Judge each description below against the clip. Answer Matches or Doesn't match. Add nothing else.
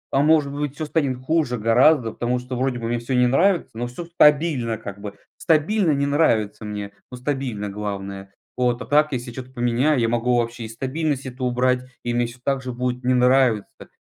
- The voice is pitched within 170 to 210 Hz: Doesn't match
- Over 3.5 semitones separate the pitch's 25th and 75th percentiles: Doesn't match